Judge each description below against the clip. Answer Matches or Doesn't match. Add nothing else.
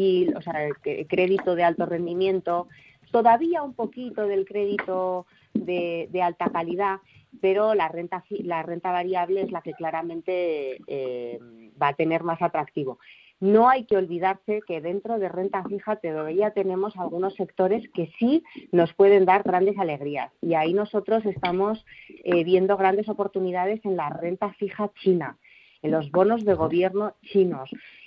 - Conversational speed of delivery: Matches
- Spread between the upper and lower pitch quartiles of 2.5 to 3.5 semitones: Matches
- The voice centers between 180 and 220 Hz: Matches